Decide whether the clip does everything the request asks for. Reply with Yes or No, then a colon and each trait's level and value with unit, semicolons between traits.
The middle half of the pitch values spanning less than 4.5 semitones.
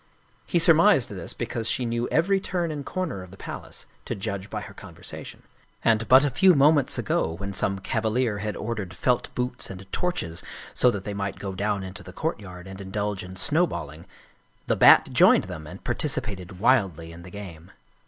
No: average, 4.9 semitones